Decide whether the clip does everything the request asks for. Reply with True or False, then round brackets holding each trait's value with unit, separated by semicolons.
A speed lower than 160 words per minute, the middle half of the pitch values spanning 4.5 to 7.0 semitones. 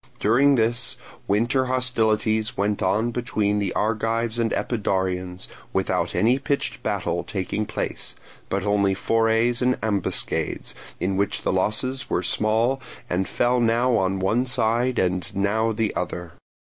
False (140 wpm; 3.2 semitones)